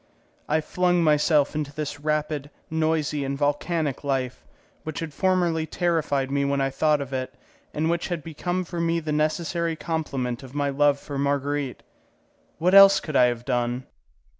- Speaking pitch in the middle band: Yes, medium, 150 Hz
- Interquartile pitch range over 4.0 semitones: No, average, 2.7 semitones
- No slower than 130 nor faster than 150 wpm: No, average, 165 wpm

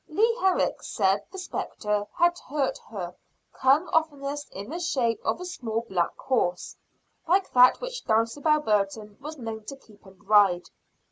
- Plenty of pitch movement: Yes, wide, 7.1 semitones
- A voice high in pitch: Yes, very high, 250 Hz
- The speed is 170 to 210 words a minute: No, average, 155 wpm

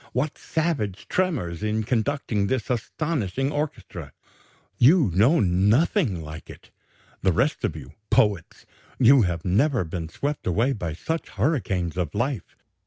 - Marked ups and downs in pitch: Yes, wide, 7.9 semitones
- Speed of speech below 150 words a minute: Yes, slow, 135 wpm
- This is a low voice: Yes, low, 110 Hz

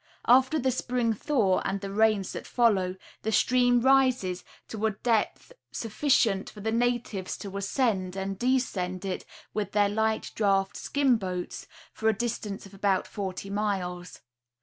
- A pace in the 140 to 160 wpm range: Yes, average, 150 wpm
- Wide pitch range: No, average, 3.8 semitones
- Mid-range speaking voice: No, high, 210 Hz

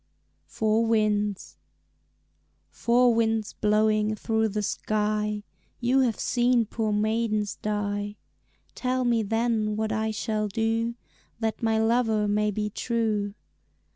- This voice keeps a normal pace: No, slow, 115 wpm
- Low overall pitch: No, high, 220 Hz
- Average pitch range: No, narrow, 1.4 semitones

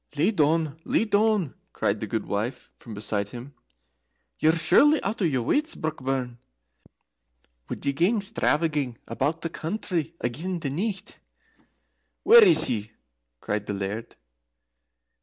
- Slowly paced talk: Yes, slow, 130 wpm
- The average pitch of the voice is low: No, medium, 155 Hz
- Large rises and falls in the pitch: Yes, wide, 7.7 semitones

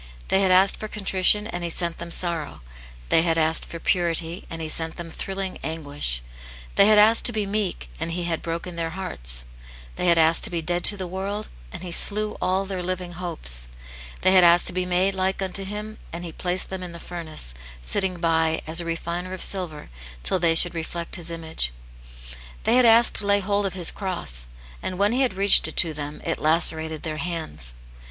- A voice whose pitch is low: No, medium, 175 Hz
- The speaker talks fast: Yes, fast, 210 wpm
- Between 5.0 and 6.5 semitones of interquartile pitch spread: No, average, 2.8 semitones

